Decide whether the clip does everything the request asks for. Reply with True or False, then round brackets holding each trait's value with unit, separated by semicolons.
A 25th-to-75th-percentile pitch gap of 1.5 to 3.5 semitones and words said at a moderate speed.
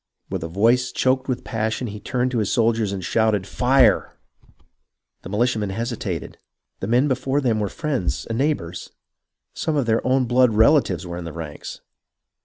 False (4.3 semitones; 180 wpm)